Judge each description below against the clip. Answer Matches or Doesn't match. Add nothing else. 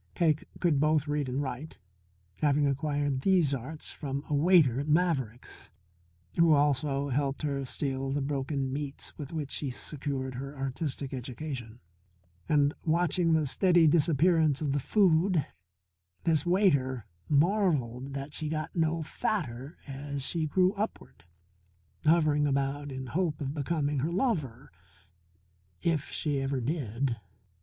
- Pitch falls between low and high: Matches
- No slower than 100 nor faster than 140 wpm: Matches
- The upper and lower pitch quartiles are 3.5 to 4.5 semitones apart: Doesn't match